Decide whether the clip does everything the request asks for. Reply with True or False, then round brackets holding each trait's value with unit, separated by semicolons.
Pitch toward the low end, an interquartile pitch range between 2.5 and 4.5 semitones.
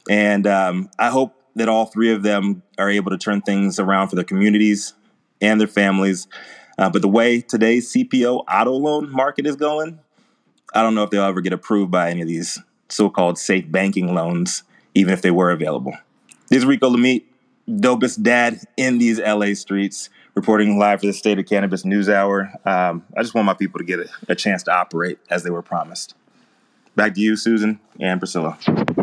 True (105 Hz; 3.5 semitones)